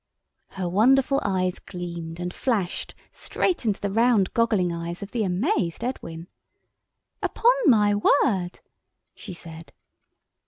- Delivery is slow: Yes, slow, 120 wpm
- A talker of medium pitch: No, high, 195 Hz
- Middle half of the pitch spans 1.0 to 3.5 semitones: No, average, 4.7 semitones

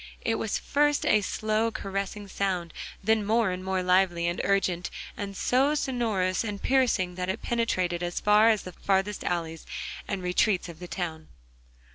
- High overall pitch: Yes, high, 195 Hz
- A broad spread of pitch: No, average, 3.4 semitones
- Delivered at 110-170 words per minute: Yes, average, 165 wpm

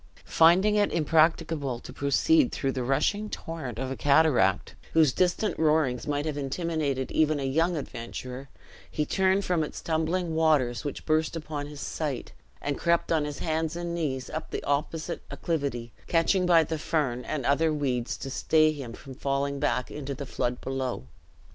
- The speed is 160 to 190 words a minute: Yes, average, 170 wpm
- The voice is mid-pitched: Yes, medium, 150 Hz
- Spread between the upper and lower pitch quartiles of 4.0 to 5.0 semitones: No, average, 3.3 semitones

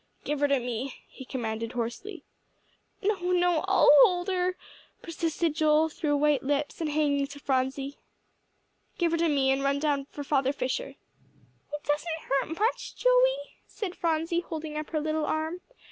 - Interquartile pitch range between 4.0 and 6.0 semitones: No, average, 3.6 semitones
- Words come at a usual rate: Yes, average, 160 wpm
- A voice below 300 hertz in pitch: No, very high, 305 Hz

